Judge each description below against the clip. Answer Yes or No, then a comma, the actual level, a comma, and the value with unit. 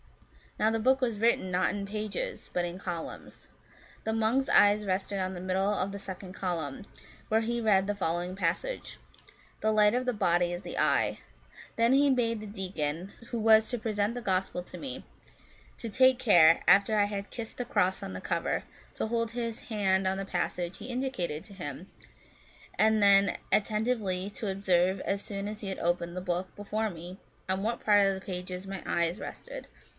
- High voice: Yes, high, 200 Hz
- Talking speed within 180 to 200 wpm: Yes, average, 195 wpm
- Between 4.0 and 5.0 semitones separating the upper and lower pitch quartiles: No, average, 3.2 semitones